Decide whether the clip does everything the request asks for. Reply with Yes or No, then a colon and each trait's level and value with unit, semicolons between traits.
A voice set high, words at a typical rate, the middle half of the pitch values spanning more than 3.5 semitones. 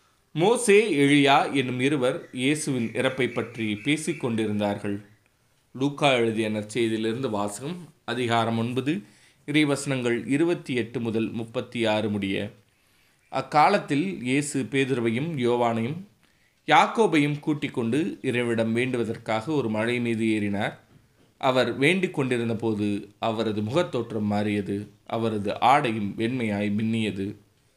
No: low, 120 Hz; average, 100 wpm; average, 3.9 semitones